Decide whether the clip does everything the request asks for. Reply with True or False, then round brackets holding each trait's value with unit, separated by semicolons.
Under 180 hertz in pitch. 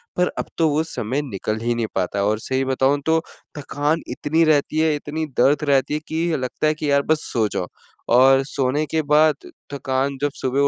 True (140 Hz)